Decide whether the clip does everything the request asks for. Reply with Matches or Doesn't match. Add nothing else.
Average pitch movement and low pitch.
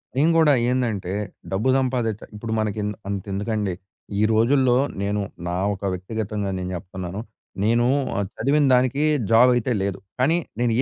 Matches